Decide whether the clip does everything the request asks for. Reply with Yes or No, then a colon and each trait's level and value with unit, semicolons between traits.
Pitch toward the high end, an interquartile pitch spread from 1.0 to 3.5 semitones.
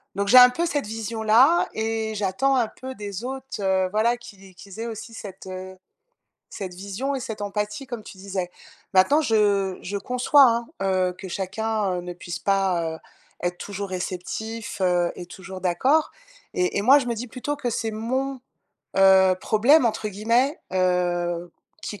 No: high, 210 Hz; average, 4.2 semitones